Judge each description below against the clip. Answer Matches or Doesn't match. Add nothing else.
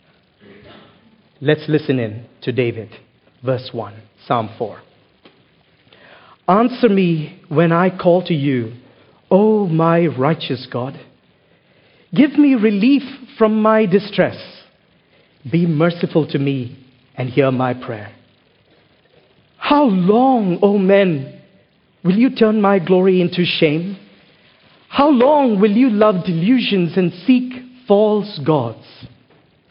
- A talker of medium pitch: Matches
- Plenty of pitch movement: Matches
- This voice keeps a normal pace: Doesn't match